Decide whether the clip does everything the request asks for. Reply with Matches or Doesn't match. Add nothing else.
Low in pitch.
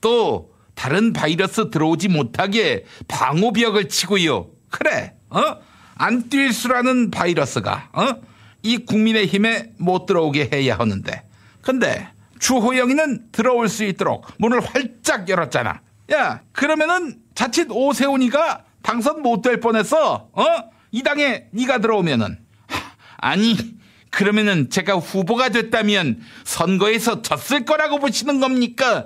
Doesn't match